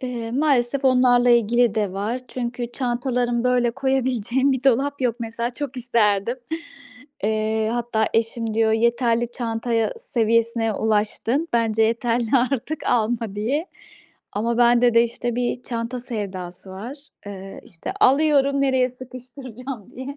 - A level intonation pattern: Yes, narrow, 2.2 semitones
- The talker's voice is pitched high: Yes, high, 240 Hz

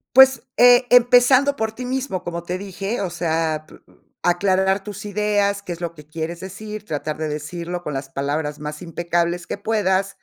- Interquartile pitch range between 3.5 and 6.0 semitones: Yes, average, 4.4 semitones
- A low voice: No, medium, 185 Hz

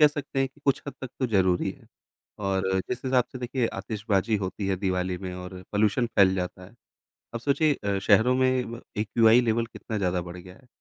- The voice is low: Yes, low, 110 Hz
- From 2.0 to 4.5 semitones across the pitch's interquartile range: No, average, 5.0 semitones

